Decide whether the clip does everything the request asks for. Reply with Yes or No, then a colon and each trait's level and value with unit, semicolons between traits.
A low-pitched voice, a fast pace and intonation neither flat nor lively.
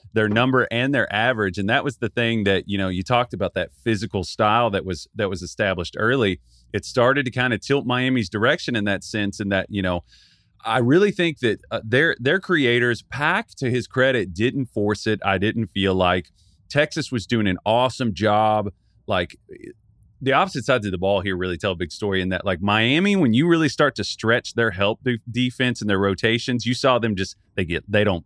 Yes: low, 110 Hz; fast, 215 wpm; average, 4.2 semitones